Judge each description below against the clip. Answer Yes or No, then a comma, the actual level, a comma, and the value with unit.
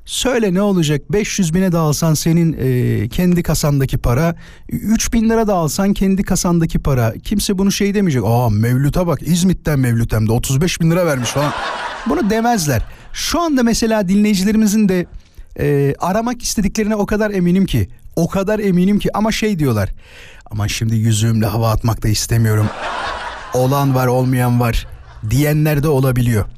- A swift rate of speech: Yes, fast, 160 wpm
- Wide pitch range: Yes, wide, 8.6 semitones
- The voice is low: No, medium, 160 Hz